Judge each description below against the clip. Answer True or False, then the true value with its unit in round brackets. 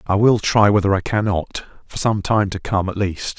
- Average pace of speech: False (230 wpm)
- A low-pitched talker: True (100 Hz)